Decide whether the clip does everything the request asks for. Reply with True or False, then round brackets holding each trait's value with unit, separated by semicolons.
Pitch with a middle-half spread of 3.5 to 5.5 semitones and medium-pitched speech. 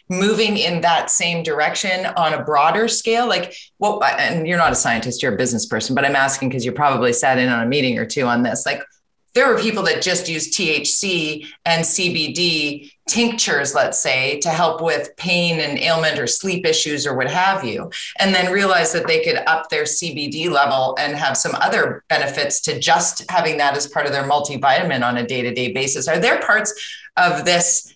True (4.2 semitones; 160 Hz)